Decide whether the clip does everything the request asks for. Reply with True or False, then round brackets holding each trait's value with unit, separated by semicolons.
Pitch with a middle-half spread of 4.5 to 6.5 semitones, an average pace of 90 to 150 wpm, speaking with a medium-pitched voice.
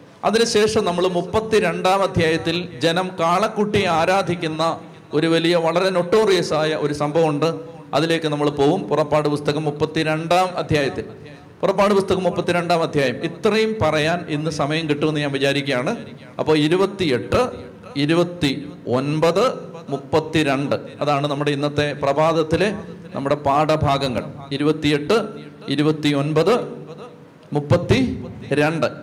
False (3.0 semitones; 105 wpm; 155 Hz)